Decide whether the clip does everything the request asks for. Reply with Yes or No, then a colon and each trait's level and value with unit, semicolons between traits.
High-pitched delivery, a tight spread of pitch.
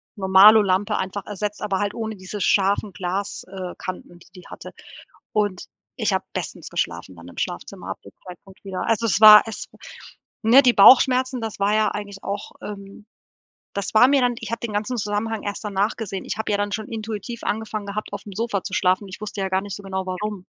Yes: high, 205 Hz; narrow, 2.2 semitones